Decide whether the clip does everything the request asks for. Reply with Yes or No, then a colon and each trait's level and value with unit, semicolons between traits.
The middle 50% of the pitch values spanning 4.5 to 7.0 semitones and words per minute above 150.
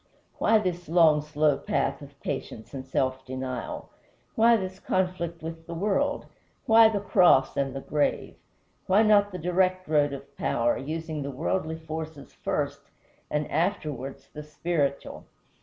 No: average, 4.8 semitones; average, 145 wpm